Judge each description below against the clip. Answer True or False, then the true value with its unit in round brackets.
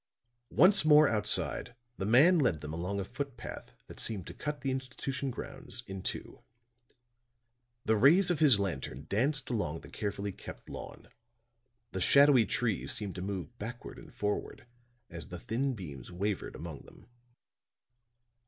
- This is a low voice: True (110 Hz)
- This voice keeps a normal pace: True (155 wpm)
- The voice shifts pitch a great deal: True (6.3 semitones)